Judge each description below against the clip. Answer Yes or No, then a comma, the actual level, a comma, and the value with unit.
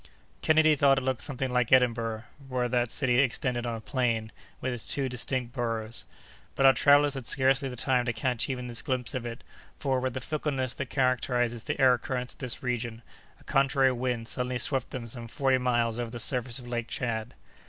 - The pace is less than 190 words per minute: No, fast, 205 wpm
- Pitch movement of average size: No, narrow, 1.9 semitones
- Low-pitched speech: Yes, low, 125 Hz